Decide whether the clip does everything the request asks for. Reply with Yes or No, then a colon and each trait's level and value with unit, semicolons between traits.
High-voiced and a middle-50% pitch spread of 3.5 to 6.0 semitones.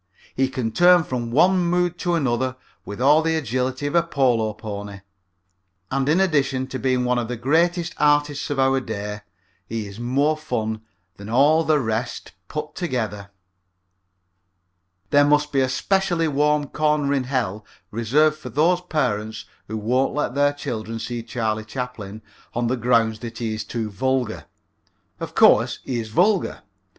No: low, 130 Hz; average, 4.9 semitones